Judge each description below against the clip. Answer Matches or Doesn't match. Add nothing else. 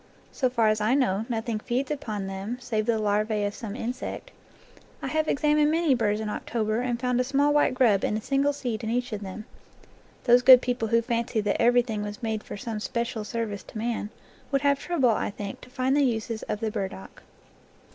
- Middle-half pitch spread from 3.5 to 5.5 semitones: Doesn't match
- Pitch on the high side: Matches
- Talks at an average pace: Doesn't match